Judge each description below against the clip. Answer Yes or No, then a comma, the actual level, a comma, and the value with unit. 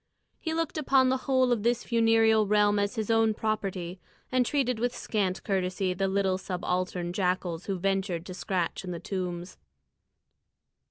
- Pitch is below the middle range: No, high, 200 Hz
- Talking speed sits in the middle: Yes, average, 160 wpm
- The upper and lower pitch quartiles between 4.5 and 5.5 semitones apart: No, average, 3.7 semitones